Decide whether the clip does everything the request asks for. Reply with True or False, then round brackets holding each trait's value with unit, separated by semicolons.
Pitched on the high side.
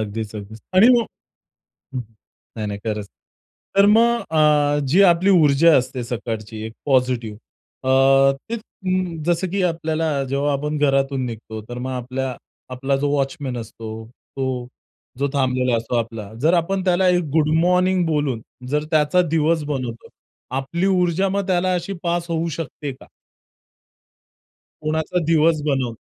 False (145 Hz)